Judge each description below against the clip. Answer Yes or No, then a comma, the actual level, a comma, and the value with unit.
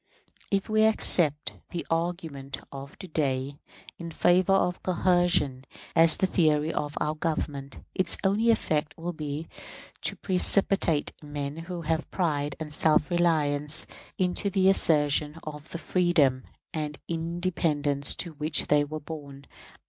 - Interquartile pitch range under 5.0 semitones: Yes, average, 3.1 semitones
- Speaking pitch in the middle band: Yes, medium, 155 Hz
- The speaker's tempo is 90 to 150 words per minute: Yes, slow, 135 wpm